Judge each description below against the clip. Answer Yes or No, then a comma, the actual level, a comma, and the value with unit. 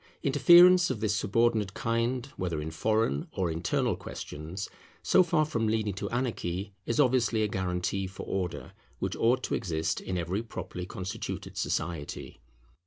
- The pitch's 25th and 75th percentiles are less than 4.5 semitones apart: No, average, 4.8 semitones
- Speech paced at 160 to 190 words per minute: No, average, 150 wpm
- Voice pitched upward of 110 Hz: No, low, 105 Hz